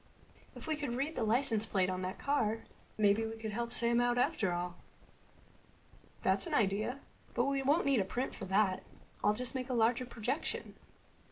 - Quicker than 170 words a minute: Yes, average, 185 wpm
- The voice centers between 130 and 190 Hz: No, high, 235 Hz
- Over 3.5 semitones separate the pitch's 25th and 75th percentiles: Yes, average, 3.9 semitones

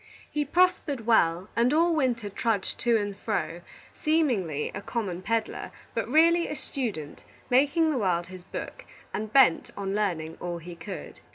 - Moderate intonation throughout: No, wide, 7.2 semitones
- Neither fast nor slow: Yes, average, 160 wpm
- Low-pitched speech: No, high, 225 Hz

